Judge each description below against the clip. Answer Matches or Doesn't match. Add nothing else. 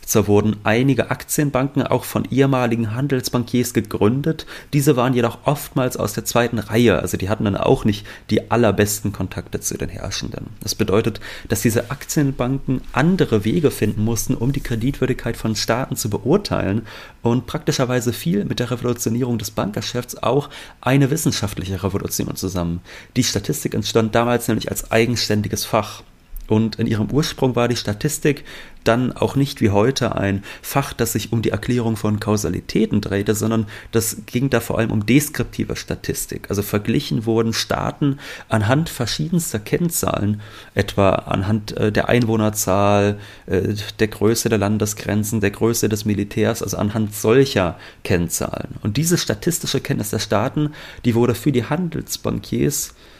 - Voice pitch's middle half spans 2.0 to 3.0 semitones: Doesn't match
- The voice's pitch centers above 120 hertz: Doesn't match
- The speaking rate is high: Doesn't match